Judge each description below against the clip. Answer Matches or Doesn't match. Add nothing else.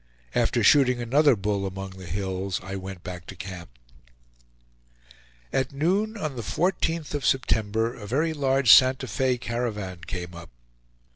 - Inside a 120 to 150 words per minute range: Matches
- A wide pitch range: Matches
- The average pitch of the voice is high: Doesn't match